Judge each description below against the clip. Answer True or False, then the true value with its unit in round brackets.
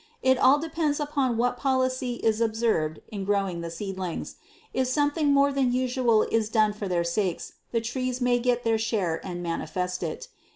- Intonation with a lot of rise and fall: False (4.9 semitones)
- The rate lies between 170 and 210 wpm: True (175 wpm)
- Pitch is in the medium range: False (230 Hz)